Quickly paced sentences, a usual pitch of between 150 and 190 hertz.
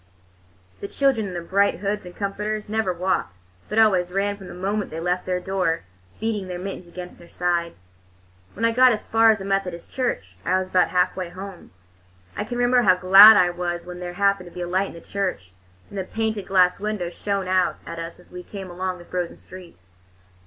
Yes: fast, 215 wpm; medium, 185 Hz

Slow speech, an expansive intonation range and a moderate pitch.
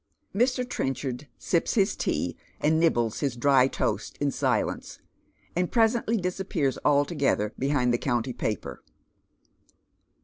Yes: slow, 115 wpm; wide, 6.5 semitones; medium, 145 Hz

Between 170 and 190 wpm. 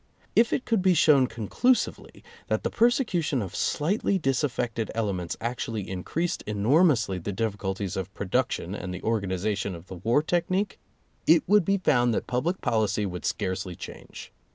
No: average, 160 wpm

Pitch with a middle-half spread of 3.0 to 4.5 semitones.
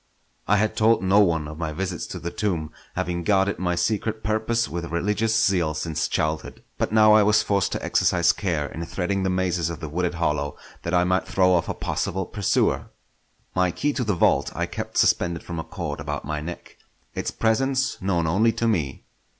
Yes: average, 4.0 semitones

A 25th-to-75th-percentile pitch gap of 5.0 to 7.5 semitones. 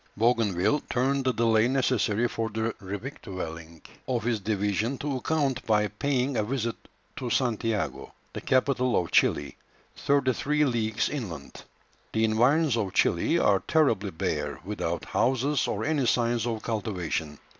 No: average, 4.0 semitones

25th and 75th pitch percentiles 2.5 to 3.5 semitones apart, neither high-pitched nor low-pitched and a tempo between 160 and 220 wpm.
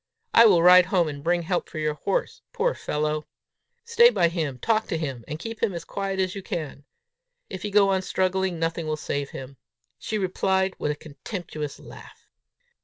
No: average, 4.2 semitones; medium, 175 Hz; average, 190 wpm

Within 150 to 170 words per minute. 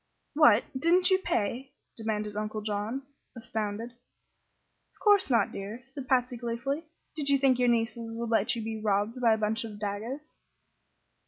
Yes: average, 160 wpm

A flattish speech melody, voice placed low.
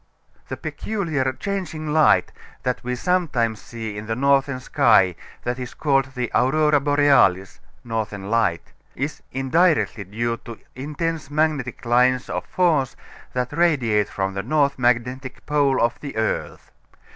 No: average, 4.1 semitones; low, 130 Hz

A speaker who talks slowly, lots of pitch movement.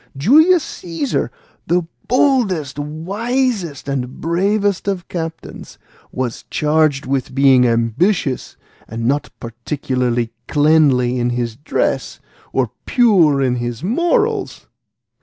Yes: slow, 100 wpm; wide, 7.8 semitones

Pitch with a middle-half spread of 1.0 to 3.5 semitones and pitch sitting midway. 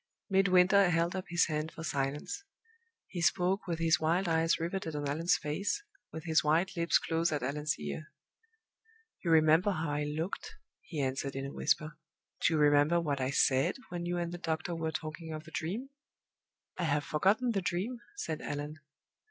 Yes: average, 2.8 semitones; medium, 160 Hz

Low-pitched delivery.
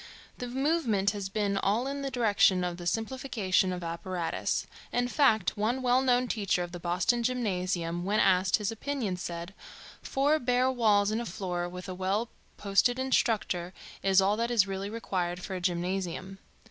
No: high, 200 Hz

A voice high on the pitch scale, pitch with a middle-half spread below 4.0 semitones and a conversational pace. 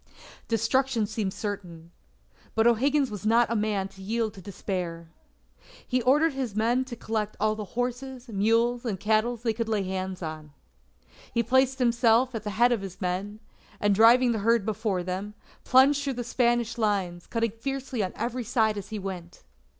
Yes: high, 220 Hz; average, 3.4 semitones; average, 175 wpm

